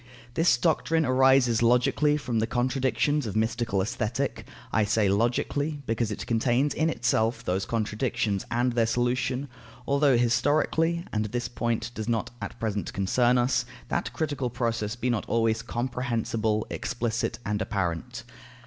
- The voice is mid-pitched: No, low, 120 Hz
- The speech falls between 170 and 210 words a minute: No, average, 140 wpm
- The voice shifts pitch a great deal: No, average, 2.8 semitones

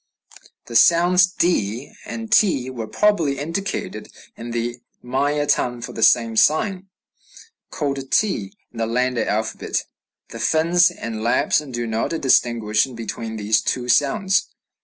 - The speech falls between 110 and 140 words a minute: Yes, slow, 135 wpm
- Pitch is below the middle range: Yes, low, 130 Hz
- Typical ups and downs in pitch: No, wide, 6.3 semitones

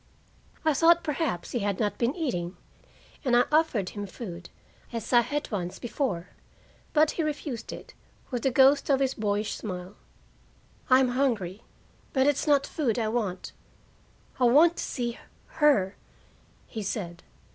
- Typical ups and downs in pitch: No, wide, 5.8 semitones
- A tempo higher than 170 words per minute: No, average, 150 wpm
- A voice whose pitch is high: Yes, high, 240 Hz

